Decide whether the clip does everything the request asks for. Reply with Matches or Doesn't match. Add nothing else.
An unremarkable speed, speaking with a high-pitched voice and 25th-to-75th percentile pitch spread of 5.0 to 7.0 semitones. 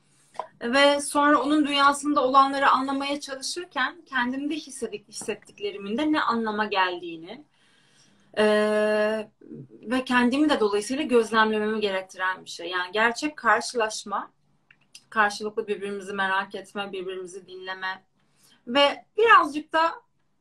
Matches